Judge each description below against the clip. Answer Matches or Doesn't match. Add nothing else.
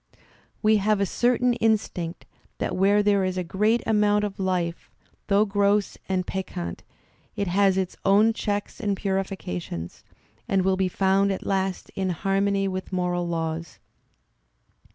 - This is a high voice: Matches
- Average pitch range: Doesn't match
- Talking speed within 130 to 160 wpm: Matches